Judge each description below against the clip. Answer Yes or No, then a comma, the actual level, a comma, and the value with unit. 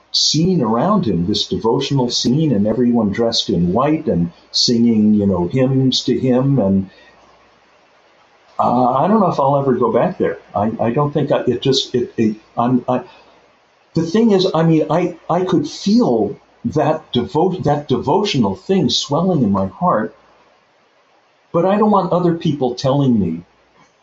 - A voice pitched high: No, low, 135 Hz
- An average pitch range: No, wide, 5.7 semitones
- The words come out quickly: No, average, 160 wpm